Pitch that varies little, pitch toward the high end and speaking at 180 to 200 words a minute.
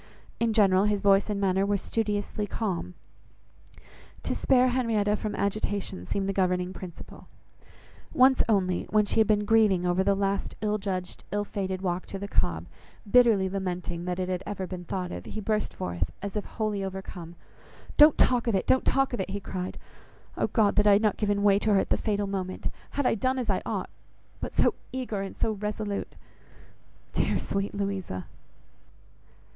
Yes: narrow, 2.2 semitones; high, 200 Hz; average, 185 wpm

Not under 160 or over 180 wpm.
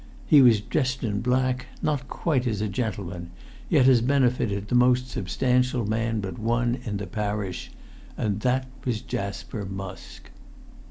No: average, 150 wpm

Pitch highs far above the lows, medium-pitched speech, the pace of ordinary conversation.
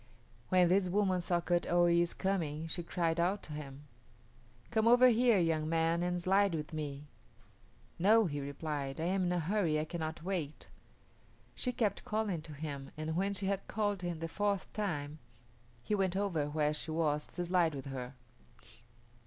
No: average, 4.0 semitones; medium, 170 Hz; average, 180 wpm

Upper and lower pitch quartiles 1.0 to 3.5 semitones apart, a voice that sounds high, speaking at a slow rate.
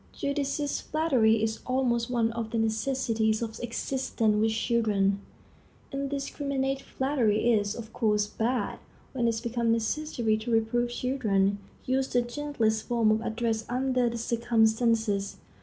Yes: average, 2.7 semitones; high, 235 Hz; slow, 130 wpm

